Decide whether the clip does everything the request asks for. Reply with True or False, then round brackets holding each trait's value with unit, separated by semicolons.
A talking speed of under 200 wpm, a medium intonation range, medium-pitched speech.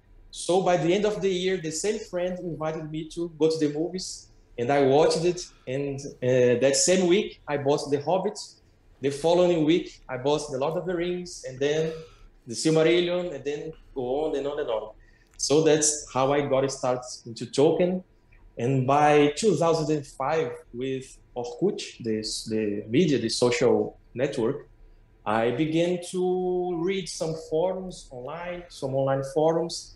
False (160 wpm; 5.8 semitones; 150 Hz)